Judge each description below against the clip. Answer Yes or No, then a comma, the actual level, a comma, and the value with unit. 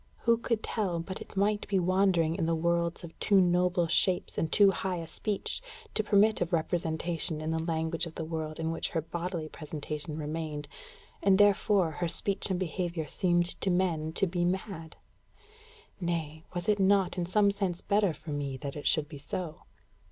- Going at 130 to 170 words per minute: No, average, 185 wpm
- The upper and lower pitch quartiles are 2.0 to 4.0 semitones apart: Yes, average, 3.1 semitones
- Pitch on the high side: No, medium, 175 Hz